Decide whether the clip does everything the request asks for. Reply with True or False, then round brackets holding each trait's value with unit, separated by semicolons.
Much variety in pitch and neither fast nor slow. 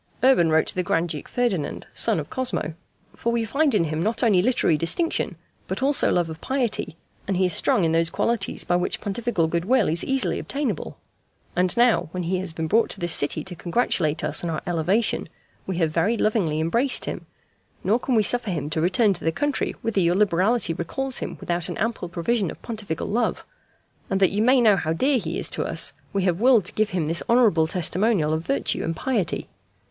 False (6.0 semitones; 215 wpm)